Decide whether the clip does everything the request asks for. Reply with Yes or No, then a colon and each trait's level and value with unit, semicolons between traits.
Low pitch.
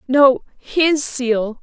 No: very high, 260 Hz